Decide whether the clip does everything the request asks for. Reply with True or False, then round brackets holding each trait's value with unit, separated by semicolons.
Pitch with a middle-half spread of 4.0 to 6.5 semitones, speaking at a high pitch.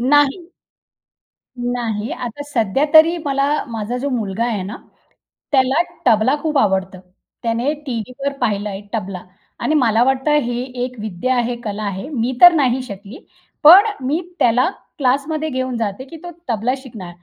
True (4.4 semitones; 245 Hz)